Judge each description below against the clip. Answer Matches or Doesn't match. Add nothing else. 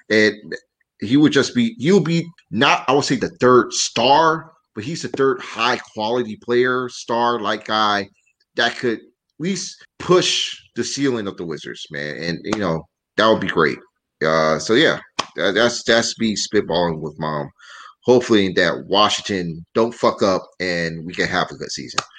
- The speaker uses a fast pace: Doesn't match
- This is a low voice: Matches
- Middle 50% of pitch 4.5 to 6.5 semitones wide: Matches